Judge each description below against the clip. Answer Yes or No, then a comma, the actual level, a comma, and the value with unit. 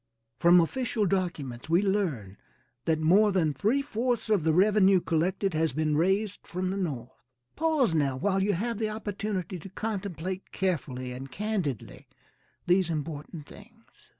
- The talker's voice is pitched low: No, medium, 185 Hz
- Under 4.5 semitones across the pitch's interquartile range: No, average, 4.8 semitones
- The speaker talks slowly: No, average, 150 wpm